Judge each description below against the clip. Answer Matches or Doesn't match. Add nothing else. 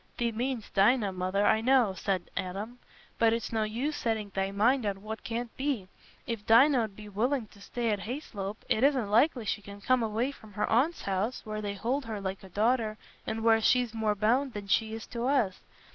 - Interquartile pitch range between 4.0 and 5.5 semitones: Doesn't match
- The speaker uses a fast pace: Matches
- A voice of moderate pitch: Doesn't match